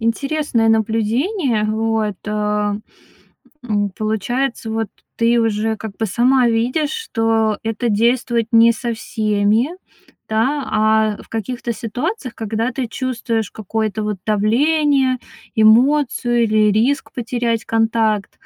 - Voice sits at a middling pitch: No, high, 225 Hz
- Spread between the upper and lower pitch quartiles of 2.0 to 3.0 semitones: Yes, narrow, 2.4 semitones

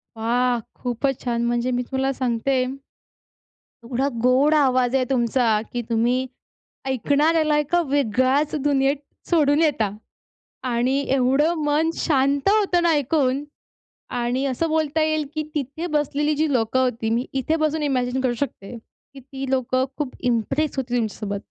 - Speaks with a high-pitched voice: Yes, very high, 265 Hz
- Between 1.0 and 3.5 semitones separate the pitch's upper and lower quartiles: Yes, average, 3.2 semitones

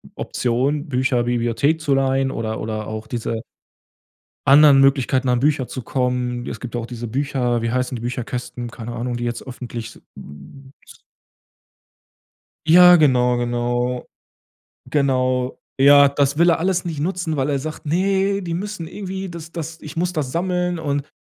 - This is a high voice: No, low, 135 Hz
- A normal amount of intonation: Yes, average, 4.5 semitones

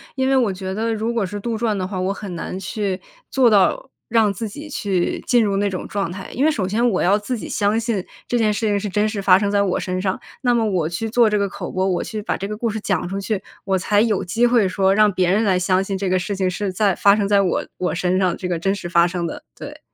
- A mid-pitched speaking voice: No, high, 200 Hz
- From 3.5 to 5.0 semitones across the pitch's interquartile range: No, average, 2.7 semitones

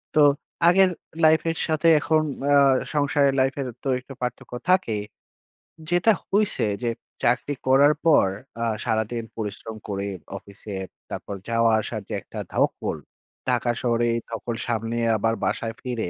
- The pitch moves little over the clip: No, average, 4.5 semitones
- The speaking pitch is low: Yes, low, 120 Hz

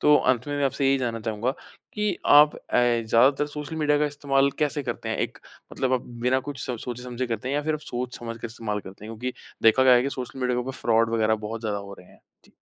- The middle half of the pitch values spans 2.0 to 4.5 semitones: Yes, average, 3.5 semitones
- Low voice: Yes, low, 125 Hz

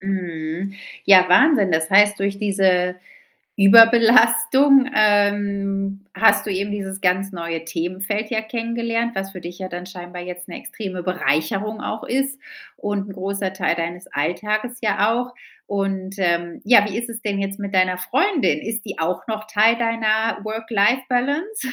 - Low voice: No, high, 200 Hz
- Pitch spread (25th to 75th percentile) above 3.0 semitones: Yes, average, 3.5 semitones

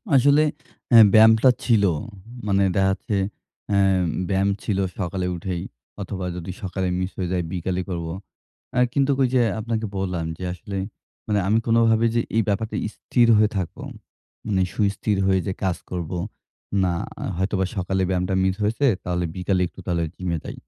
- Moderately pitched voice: No, very low, 95 Hz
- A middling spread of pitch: Yes, average, 3.2 semitones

